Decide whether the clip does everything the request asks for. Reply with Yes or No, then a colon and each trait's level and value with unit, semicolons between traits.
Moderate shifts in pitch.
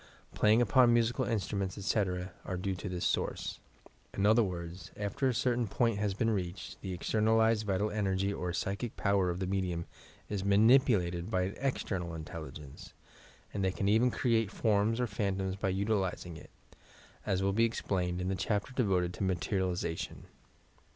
Yes: average, 3.3 semitones